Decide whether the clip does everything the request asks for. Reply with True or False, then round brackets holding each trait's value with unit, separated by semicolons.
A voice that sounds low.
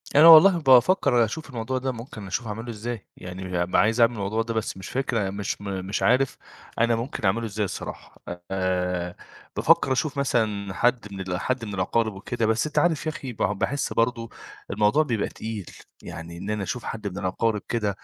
True (110 Hz)